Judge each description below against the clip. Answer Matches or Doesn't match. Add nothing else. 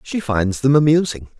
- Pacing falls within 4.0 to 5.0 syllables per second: Matches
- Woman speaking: Doesn't match